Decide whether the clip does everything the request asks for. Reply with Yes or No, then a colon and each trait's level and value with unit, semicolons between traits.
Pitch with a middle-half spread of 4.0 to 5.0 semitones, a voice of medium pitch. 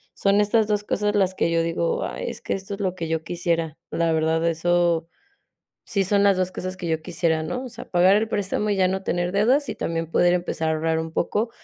No: average, 3.4 semitones; medium, 180 Hz